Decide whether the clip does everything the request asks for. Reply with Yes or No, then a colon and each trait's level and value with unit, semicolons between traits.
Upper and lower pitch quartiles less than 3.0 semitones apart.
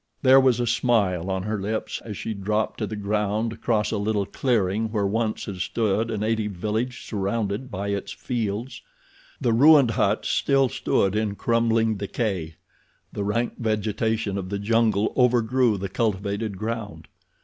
Yes: narrow, 2.5 semitones